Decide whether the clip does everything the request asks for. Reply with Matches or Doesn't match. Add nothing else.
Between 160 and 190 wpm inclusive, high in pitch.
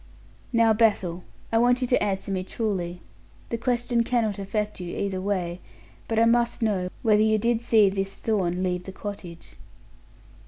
Matches